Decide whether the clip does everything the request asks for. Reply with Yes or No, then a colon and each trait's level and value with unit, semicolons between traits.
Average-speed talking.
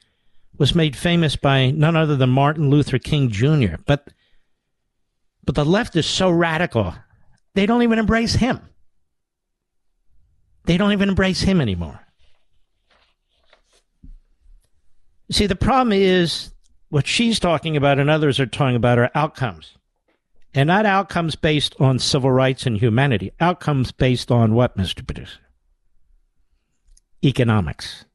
No: slow, 130 wpm